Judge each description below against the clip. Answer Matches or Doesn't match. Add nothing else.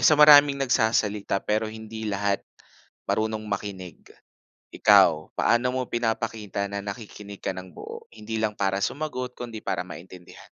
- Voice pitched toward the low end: Matches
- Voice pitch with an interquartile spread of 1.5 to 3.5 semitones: Matches